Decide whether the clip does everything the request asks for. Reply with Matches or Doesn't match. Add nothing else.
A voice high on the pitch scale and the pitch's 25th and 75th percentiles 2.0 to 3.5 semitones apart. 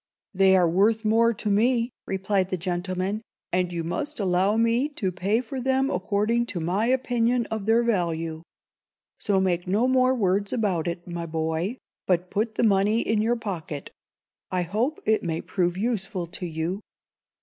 Doesn't match